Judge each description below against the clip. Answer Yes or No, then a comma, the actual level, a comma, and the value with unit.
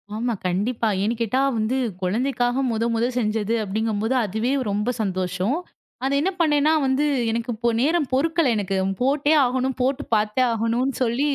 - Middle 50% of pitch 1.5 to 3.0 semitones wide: No, average, 3.7 semitones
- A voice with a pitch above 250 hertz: No, high, 235 Hz